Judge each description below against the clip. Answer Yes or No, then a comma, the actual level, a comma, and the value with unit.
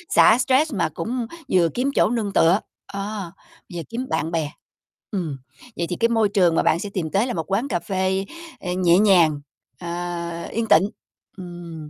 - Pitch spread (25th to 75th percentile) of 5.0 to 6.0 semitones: No, average, 4.1 semitones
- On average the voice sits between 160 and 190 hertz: Yes, medium, 185 Hz